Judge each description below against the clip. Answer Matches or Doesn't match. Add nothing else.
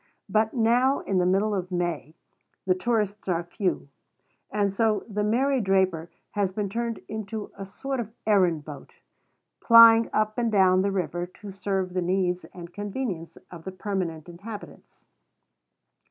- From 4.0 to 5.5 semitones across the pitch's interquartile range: Doesn't match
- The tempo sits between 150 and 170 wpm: Matches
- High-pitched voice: Matches